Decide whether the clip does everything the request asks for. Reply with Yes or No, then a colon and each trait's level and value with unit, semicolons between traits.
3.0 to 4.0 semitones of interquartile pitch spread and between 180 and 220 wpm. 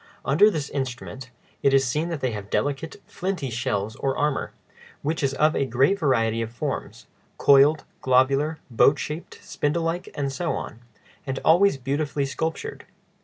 No: average, 3.3 semitones; average, 150 wpm